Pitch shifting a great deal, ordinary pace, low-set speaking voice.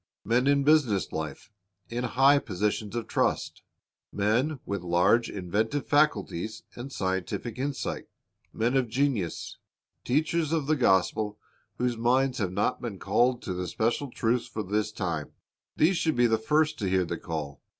Yes: wide, 5.8 semitones; average, 160 wpm; low, 115 Hz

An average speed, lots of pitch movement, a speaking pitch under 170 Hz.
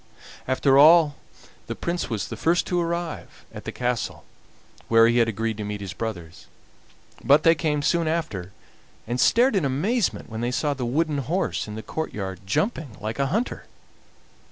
Yes: average, 175 wpm; wide, 6.7 semitones; medium, 140 Hz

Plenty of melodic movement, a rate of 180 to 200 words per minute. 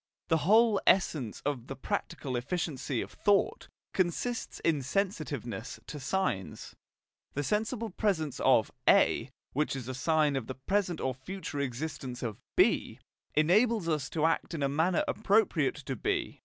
No: wide, 6.4 semitones; average, 150 wpm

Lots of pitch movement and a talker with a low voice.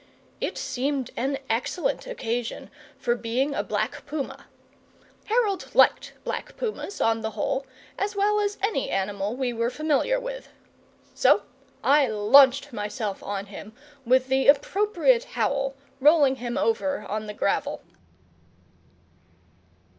No: wide, 7.3 semitones; very high, 270 Hz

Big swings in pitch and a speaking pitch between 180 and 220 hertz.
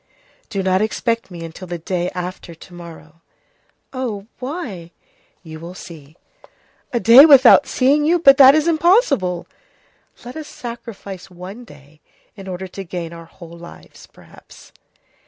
Yes: wide, 6.9 semitones; high, 190 Hz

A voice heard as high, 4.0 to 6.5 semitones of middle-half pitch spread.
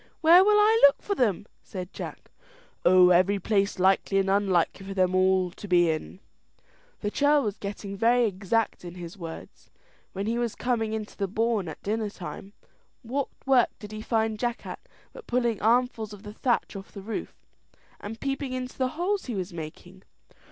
Yes: high, 210 Hz; average, 4.3 semitones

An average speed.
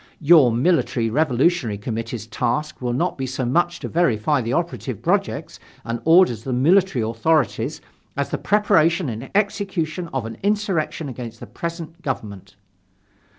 Yes: average, 150 wpm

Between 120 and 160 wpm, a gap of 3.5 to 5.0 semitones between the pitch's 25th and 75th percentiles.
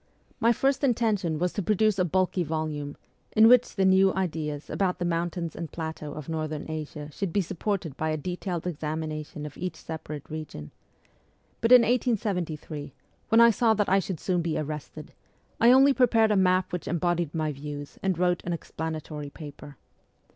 No: average, 175 wpm; average, 4.2 semitones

